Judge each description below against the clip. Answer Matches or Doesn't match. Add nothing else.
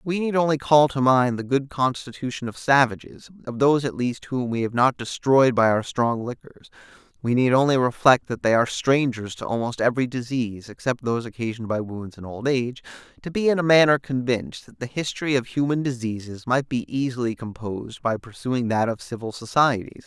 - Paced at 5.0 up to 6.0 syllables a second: Matches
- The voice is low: Matches